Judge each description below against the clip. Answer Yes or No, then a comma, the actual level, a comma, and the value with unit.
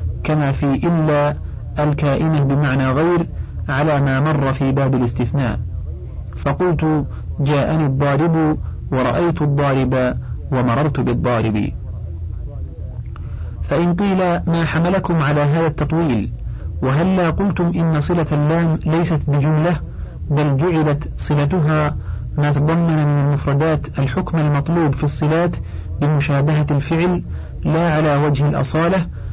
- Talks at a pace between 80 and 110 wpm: Yes, average, 100 wpm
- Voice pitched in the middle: Yes, medium, 145 Hz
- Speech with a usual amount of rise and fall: Yes, average, 3.7 semitones